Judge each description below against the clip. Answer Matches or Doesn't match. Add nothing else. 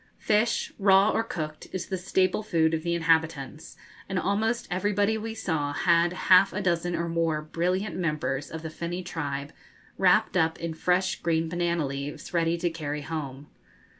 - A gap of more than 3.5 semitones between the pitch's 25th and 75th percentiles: Doesn't match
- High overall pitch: Doesn't match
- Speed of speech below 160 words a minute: Doesn't match